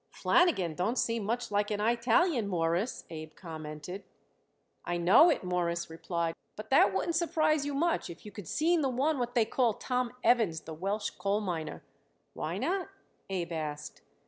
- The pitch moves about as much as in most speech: No, wide, 6.8 semitones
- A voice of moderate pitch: No, high, 205 Hz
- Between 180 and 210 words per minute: No, average, 170 wpm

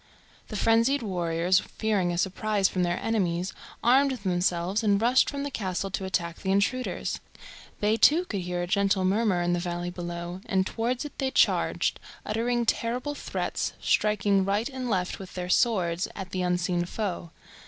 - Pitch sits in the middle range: No, high, 195 Hz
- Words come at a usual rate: Yes, average, 170 wpm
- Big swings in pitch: No, average, 4.2 semitones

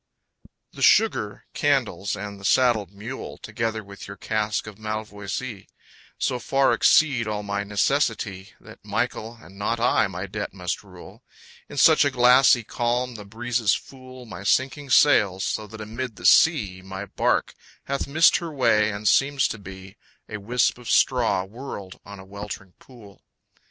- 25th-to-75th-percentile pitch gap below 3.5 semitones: No, average, 3.9 semitones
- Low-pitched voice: Yes, low, 110 Hz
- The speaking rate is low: No, average, 160 wpm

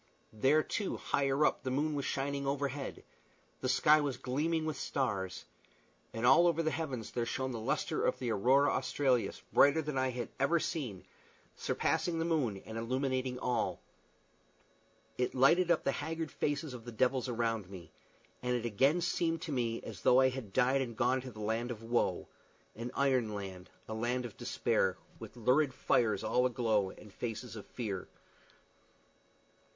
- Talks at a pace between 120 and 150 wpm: No, average, 175 wpm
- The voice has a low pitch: Yes, low, 130 Hz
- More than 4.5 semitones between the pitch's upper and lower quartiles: No, average, 3.6 semitones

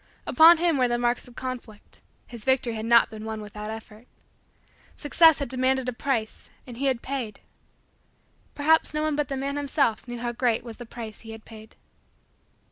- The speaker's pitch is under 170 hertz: No, high, 245 Hz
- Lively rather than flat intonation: No, average, 3.7 semitones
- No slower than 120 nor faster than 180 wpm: No, average, 195 wpm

